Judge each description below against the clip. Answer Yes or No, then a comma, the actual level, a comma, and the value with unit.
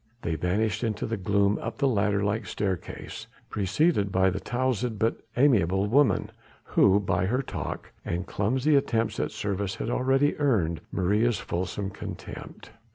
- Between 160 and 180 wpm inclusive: No, average, 150 wpm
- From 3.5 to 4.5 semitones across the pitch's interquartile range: Yes, average, 4.0 semitones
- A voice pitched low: Yes, low, 105 Hz